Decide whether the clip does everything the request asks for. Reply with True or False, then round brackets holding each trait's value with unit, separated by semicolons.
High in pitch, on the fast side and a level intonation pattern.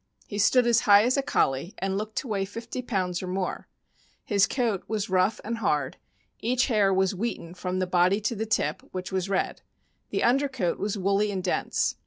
False (200 Hz; 210 wpm; 3.6 semitones)